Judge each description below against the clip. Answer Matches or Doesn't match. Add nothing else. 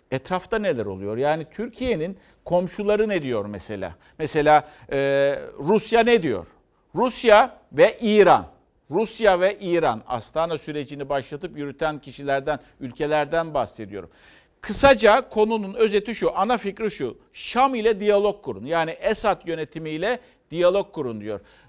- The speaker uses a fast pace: Doesn't match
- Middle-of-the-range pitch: Matches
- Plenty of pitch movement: Matches